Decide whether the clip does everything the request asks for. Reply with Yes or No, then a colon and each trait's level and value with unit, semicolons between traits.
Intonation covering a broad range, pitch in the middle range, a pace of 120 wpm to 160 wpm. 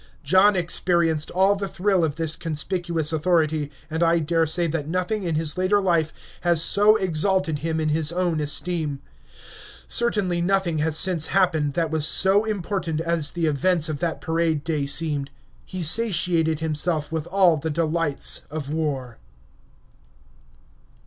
No: average, 2.8 semitones; medium, 165 Hz; average, 150 wpm